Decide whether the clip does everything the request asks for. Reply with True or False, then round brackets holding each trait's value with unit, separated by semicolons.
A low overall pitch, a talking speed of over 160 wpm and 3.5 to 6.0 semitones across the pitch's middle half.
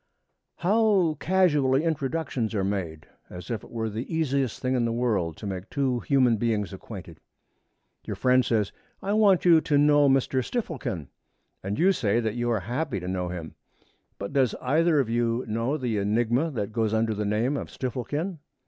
True (120 Hz; 180 wpm; 5.5 semitones)